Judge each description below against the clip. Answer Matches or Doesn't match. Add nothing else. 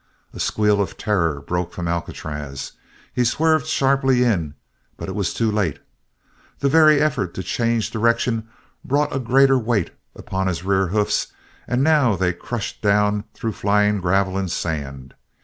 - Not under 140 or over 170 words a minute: Matches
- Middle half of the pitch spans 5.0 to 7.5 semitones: Matches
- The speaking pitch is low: Matches